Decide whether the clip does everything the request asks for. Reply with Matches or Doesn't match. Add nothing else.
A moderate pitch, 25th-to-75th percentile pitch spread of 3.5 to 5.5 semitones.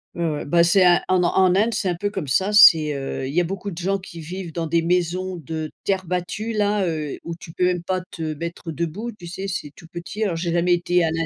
Doesn't match